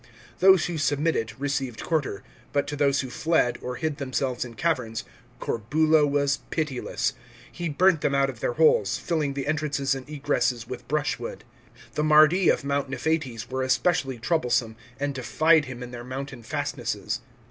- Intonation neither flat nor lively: Yes, average, 3.3 semitones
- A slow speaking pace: No, average, 165 wpm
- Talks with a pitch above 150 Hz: No, medium, 140 Hz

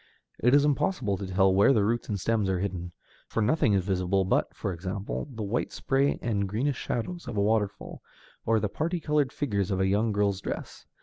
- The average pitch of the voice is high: No, low, 105 Hz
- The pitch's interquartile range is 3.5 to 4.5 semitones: Yes, average, 4.2 semitones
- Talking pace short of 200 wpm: No, fast, 205 wpm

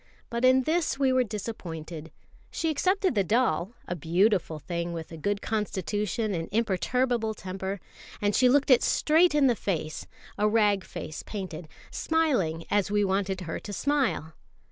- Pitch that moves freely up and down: Yes, wide, 6.2 semitones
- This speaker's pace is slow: No, average, 160 wpm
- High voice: Yes, high, 205 Hz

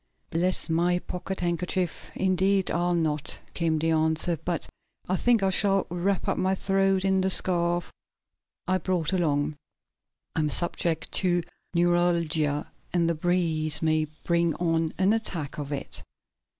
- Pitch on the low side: No, medium, 175 Hz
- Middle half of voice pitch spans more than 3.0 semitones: No, narrow, 2.6 semitones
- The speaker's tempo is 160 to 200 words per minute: No, average, 145 wpm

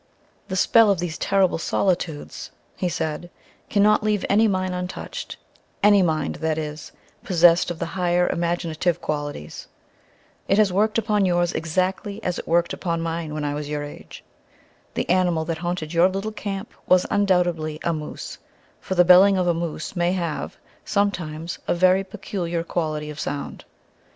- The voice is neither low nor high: Yes, medium, 175 Hz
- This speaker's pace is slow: No, average, 165 wpm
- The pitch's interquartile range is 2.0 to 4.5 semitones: Yes, average, 3.0 semitones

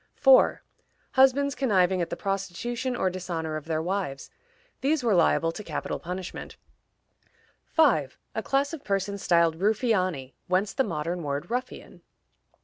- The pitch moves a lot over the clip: Yes, wide, 6.4 semitones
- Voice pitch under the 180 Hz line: No, high, 190 Hz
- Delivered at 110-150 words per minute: Yes, average, 140 wpm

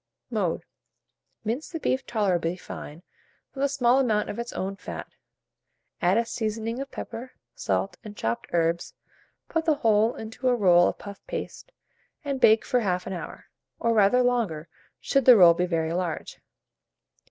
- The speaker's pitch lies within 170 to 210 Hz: No, high, 220 Hz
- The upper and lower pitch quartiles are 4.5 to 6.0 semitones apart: Yes, wide, 5.6 semitones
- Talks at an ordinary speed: Yes, average, 160 wpm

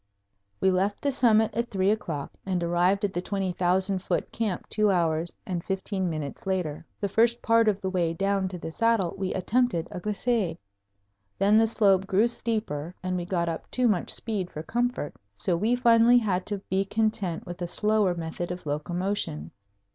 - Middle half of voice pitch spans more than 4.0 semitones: No, average, 3.7 semitones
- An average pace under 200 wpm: Yes, average, 185 wpm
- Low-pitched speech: No, high, 190 Hz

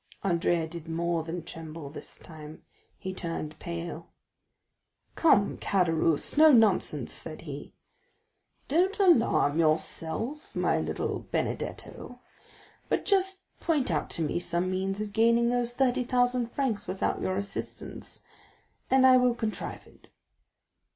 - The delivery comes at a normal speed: No, slow, 125 wpm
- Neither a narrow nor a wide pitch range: No, wide, 7.0 semitones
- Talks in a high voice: Yes, high, 195 Hz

